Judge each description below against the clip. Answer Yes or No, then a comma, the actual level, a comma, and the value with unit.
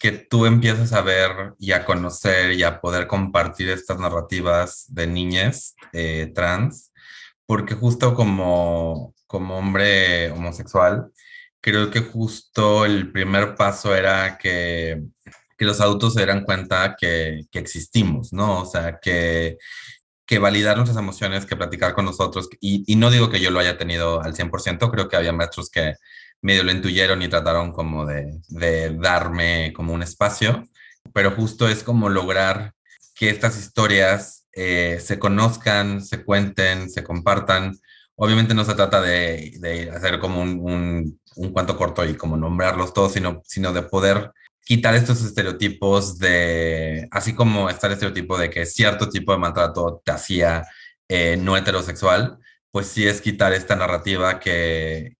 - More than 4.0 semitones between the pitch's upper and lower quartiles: No, average, 3.3 semitones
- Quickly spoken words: No, average, 155 wpm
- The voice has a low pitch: Yes, very low, 95 Hz